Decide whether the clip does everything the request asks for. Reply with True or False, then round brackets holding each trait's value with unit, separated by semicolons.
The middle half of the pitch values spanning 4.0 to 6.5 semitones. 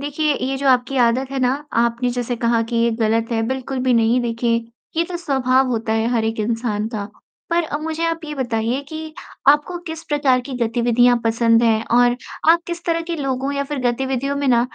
False (3.5 semitones)